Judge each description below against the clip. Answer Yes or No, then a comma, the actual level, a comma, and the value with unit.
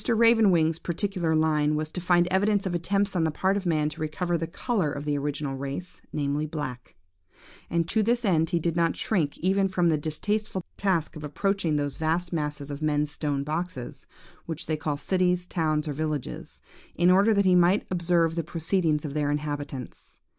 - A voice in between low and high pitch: Yes, medium, 165 Hz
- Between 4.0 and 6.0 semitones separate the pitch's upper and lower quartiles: No, average, 3.4 semitones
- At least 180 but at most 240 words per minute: Yes, average, 190 wpm